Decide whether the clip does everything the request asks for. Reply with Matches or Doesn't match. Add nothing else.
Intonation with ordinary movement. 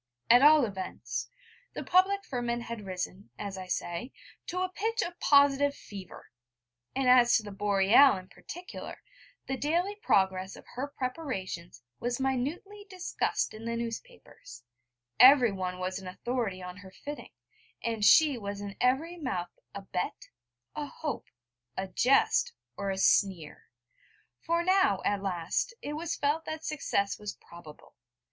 Doesn't match